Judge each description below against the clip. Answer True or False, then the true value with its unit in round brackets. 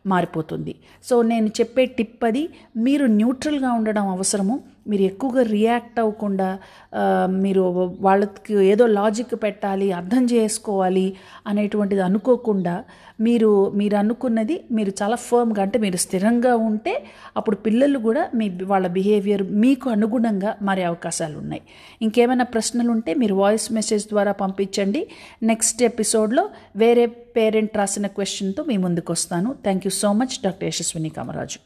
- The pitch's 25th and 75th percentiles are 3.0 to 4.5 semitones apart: True (3.4 semitones)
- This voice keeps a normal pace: False (130 wpm)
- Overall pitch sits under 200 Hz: False (215 Hz)